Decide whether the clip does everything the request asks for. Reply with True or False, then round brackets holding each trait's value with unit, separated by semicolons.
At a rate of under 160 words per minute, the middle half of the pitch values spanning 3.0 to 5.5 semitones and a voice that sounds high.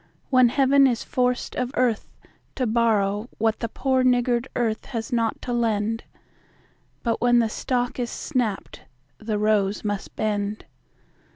False (145 wpm; 2.5 semitones; 235 Hz)